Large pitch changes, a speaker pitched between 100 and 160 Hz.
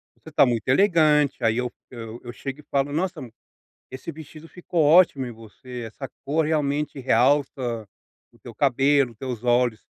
No: average, 3.8 semitones; low, 135 Hz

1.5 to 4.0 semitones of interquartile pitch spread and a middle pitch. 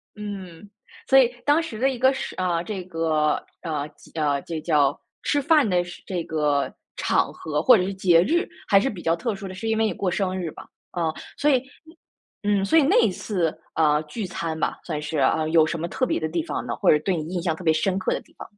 No: average, 5.0 semitones; medium, 180 Hz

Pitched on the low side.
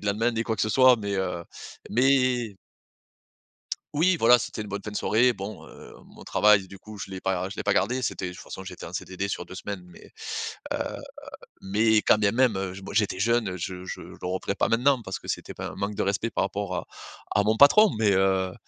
Yes: low, 105 Hz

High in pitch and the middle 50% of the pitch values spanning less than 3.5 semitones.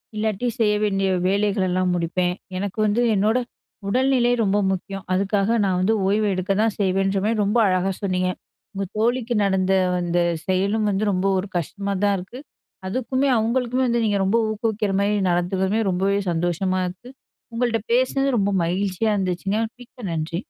Yes: high, 200 Hz; average, 3.1 semitones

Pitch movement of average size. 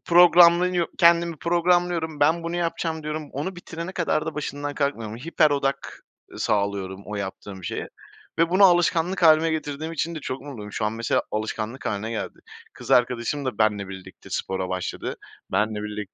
No: wide, 7.7 semitones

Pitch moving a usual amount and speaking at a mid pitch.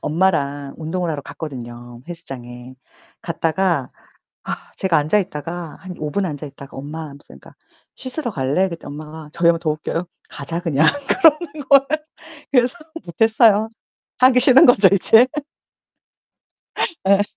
No: wide, 5.9 semitones; medium, 165 Hz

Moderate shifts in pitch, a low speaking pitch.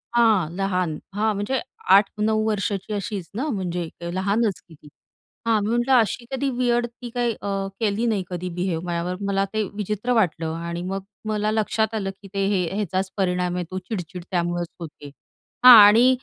No: average, 3.5 semitones; high, 200 Hz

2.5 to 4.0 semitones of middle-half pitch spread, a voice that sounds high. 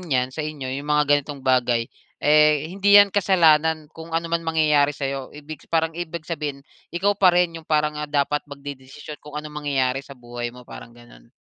No: average, 2.9 semitones; medium, 150 Hz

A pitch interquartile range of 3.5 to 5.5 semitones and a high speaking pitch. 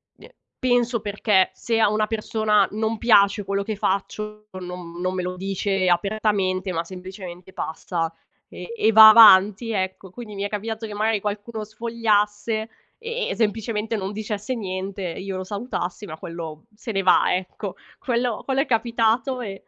No: average, 2.9 semitones; high, 210 Hz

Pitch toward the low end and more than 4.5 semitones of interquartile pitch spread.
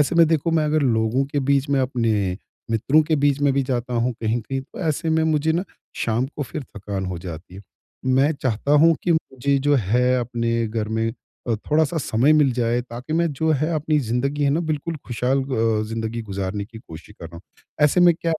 Yes: low, 130 Hz; average, 5.1 semitones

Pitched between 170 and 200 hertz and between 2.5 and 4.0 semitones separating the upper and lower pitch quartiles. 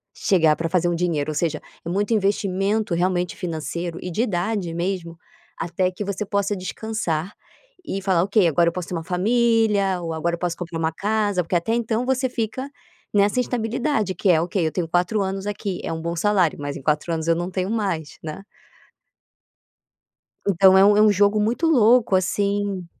Yes: high, 190 Hz; average, 3.6 semitones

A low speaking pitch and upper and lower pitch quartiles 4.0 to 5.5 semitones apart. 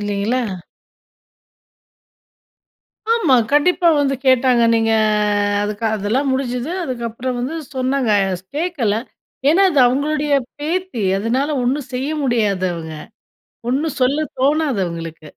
No: very high, 255 Hz; average, 4.5 semitones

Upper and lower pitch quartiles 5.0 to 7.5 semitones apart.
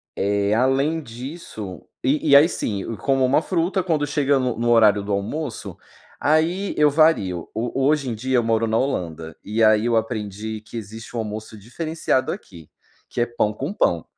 Yes: wide, 5.4 semitones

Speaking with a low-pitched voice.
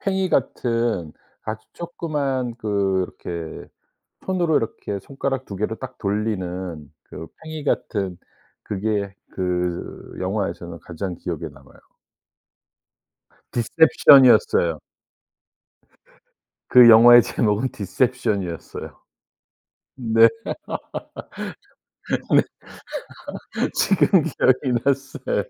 Yes: low, 110 Hz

